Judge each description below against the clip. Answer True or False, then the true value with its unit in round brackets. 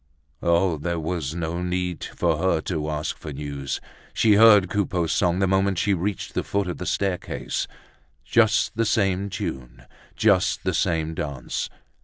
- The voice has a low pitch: True (90 Hz)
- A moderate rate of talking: True (160 wpm)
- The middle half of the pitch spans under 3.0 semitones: False (3.5 semitones)